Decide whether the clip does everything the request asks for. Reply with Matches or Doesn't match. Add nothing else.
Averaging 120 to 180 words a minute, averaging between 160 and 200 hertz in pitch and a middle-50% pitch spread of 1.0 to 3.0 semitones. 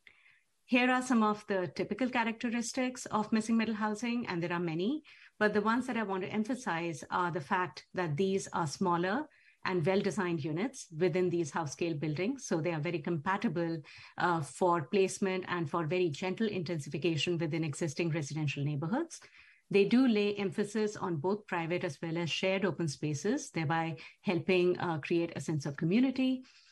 Doesn't match